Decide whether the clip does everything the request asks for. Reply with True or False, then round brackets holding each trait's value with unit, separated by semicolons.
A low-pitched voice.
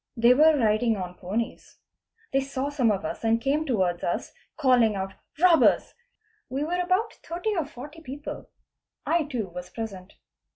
False (255 Hz)